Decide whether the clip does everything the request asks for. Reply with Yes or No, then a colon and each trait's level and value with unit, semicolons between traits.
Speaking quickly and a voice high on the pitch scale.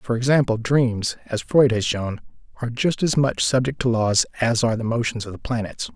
No: fast, 210 wpm; low, 120 Hz